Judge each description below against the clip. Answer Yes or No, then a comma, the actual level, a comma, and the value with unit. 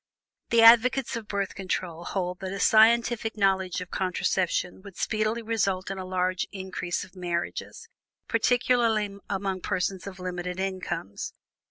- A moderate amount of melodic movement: Yes, average, 3.0 semitones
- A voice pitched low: No, high, 190 Hz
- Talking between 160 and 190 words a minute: No, average, 140 wpm